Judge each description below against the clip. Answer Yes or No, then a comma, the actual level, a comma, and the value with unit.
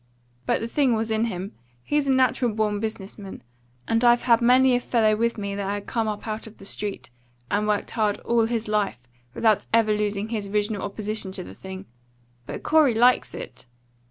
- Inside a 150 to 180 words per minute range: No, average, 200 wpm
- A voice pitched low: No, high, 220 Hz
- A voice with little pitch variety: Yes, narrow, 2.2 semitones